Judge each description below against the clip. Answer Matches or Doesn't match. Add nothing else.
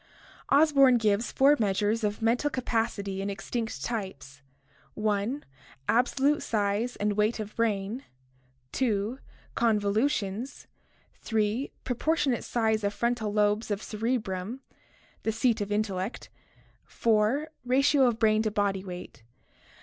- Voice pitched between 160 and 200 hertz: Doesn't match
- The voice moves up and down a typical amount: Matches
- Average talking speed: Doesn't match